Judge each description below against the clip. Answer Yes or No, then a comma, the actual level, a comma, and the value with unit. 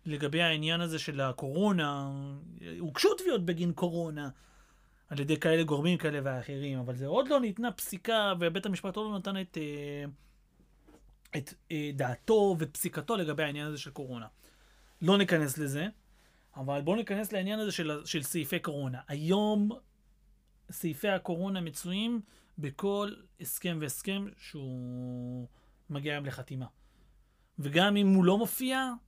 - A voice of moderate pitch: Yes, medium, 165 Hz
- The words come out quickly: No, average, 130 wpm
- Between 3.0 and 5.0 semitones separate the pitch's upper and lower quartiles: No, wide, 5.4 semitones